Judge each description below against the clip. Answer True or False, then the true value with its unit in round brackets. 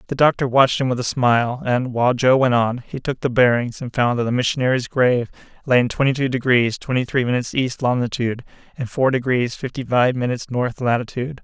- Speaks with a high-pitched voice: False (125 Hz)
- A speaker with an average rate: False (210 wpm)